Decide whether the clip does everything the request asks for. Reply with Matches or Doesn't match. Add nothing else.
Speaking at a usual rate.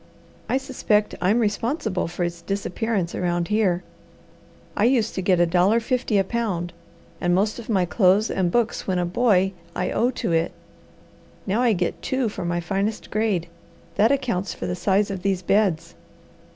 Matches